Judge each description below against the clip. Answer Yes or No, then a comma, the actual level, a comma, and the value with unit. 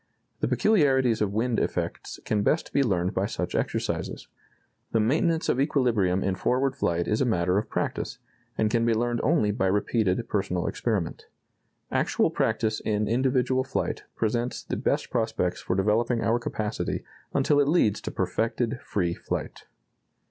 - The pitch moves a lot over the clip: No, average, 3.9 semitones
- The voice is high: No, low, 115 Hz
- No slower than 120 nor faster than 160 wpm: Yes, average, 155 wpm